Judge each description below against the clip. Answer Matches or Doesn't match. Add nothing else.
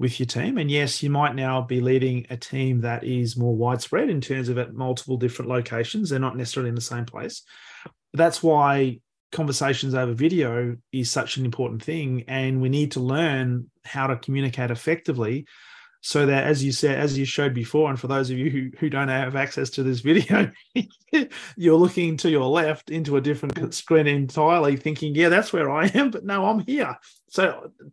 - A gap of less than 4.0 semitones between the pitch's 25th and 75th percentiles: Matches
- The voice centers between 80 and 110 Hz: Doesn't match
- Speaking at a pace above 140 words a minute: Matches